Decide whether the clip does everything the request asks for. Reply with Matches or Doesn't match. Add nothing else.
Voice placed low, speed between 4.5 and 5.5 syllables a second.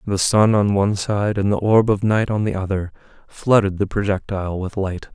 Matches